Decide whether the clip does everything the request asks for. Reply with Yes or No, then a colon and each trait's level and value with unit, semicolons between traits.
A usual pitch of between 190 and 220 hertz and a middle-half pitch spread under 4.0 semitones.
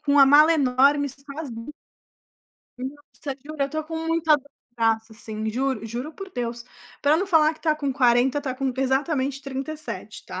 No: very high, 275 Hz; average, 3.3 semitones